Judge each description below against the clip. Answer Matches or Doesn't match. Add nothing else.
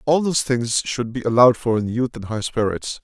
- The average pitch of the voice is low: Matches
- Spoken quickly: Matches